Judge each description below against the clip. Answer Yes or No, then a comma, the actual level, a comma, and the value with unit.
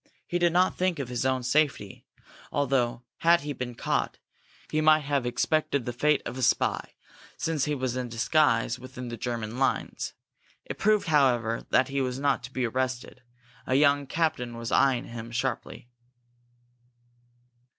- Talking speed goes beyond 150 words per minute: Yes, average, 160 wpm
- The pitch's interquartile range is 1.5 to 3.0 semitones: No, average, 3.4 semitones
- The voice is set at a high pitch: No, low, 130 Hz